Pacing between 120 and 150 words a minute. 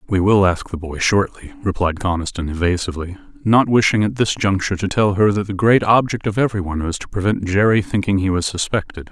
No: fast, 205 wpm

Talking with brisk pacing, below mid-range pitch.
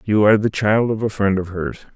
Yes: fast, 275 wpm; low, 105 Hz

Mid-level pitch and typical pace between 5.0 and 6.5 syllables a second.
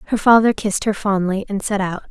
No: high, 200 Hz; 6.2 syllables/s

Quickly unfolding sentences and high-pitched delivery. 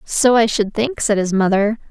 Yes: fast, 220 wpm; high, 215 Hz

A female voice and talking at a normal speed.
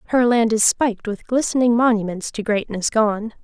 Yes: female; average, 175 wpm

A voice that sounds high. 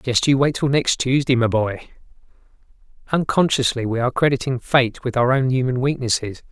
No: low, 130 Hz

